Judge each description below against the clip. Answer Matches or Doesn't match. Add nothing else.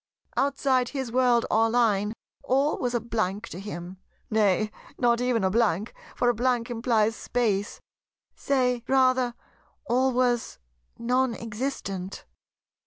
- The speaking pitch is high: Matches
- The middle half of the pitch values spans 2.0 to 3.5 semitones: Matches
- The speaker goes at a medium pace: Doesn't match